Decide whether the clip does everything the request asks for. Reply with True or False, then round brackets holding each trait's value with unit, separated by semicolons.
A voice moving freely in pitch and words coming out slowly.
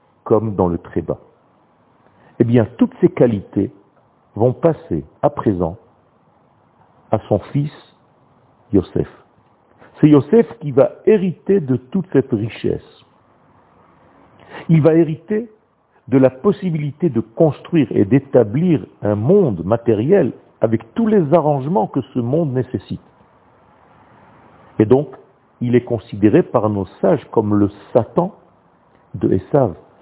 True (6.6 semitones; 120 wpm)